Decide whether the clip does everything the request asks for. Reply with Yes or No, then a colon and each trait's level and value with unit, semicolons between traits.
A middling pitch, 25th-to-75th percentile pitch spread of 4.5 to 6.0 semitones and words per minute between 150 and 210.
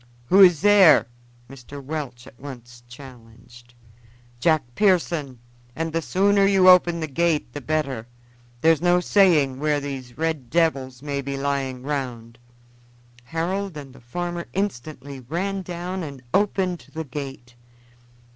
No: medium, 150 Hz; average, 5.1 semitones; slow, 135 wpm